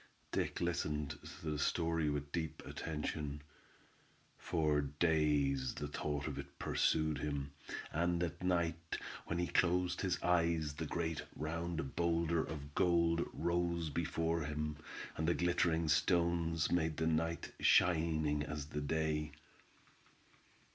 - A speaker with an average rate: No, slow, 125 wpm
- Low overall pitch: Yes, very low, 80 Hz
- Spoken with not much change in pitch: Yes, narrow, 2.2 semitones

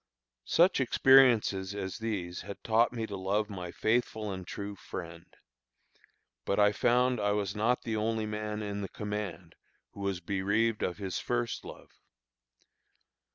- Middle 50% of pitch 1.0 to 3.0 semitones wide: Yes, average, 2.7 semitones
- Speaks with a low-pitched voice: Yes, low, 105 Hz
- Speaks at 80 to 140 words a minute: No, average, 150 wpm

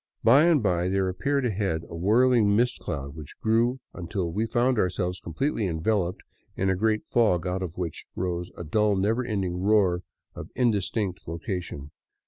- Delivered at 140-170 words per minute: Yes, average, 165 wpm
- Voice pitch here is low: Yes, very low, 95 Hz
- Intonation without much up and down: No, average, 4.2 semitones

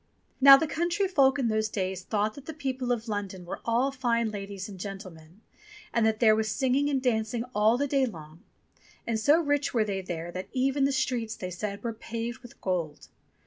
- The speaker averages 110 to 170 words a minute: No, fast, 205 wpm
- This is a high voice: Yes, high, 225 Hz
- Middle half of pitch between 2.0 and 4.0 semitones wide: No, average, 5.0 semitones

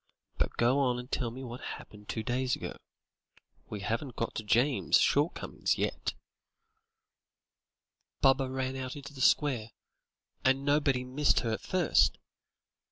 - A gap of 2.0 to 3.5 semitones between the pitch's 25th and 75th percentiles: Yes, narrow, 2.5 semitones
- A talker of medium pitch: No, low, 130 Hz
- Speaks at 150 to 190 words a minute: No, average, 140 wpm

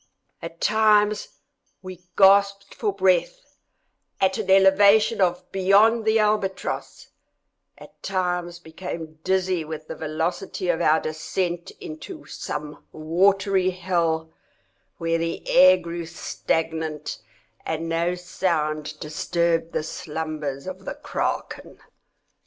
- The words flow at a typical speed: No, slow, 105 wpm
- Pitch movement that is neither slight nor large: Yes, average, 3.2 semitones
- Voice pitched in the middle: Yes, medium, 175 Hz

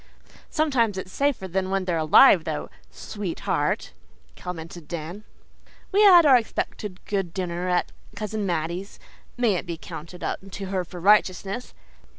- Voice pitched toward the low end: No, high, 190 Hz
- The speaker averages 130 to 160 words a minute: Yes, average, 140 wpm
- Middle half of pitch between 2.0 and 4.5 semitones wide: Yes, average, 3.5 semitones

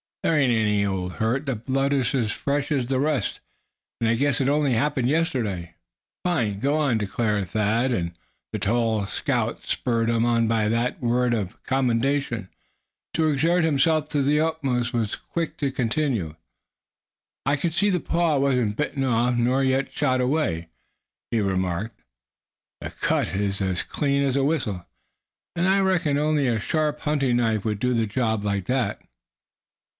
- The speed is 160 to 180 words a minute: Yes, average, 170 wpm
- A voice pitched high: No, low, 125 Hz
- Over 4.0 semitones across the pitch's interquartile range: Yes, average, 4.7 semitones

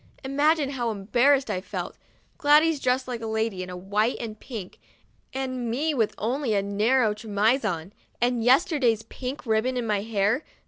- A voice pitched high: Yes, high, 235 Hz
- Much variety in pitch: No, average, 3.9 semitones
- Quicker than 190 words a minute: No, average, 165 wpm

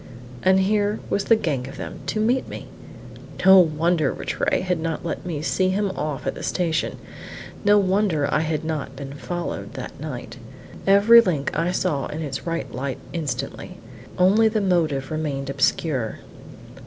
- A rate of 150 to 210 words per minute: Yes, average, 165 wpm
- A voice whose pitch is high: No, medium, 165 Hz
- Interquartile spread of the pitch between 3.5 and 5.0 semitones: Yes, average, 4.7 semitones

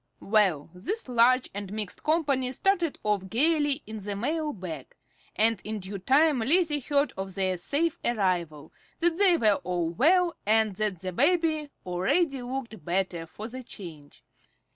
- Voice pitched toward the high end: Yes, high, 225 Hz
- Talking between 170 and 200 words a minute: No, average, 155 wpm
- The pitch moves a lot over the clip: Yes, wide, 7.7 semitones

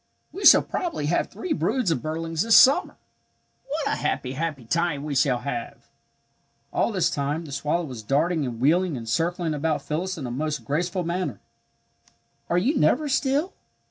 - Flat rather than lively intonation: No, average, 4.4 semitones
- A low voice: No, medium, 165 Hz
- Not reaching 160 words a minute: No, average, 175 wpm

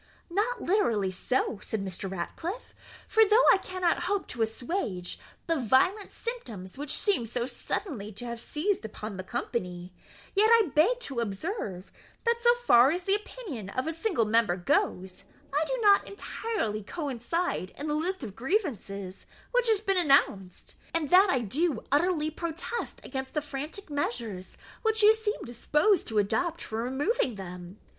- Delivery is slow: No, average, 160 wpm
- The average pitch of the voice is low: No, very high, 290 Hz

